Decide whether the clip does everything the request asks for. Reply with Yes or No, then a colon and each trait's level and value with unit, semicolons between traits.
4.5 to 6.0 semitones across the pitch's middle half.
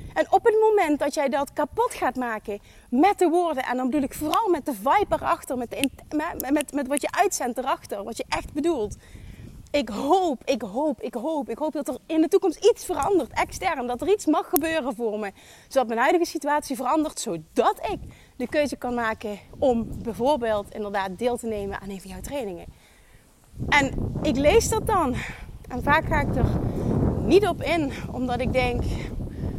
Yes: wide, 5.6 semitones